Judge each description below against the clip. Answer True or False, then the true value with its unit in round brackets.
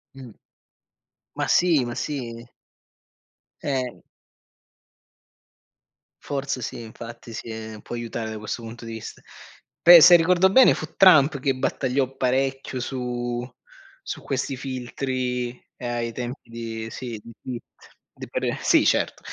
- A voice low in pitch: True (125 Hz)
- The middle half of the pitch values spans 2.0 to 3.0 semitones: True (2.6 semitones)